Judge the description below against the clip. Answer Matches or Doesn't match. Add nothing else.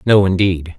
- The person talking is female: Doesn't match